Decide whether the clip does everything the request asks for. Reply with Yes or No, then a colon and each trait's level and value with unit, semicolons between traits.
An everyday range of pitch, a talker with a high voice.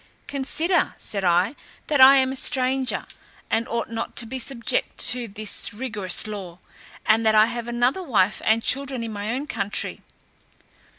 Yes: average, 3.5 semitones; high, 235 Hz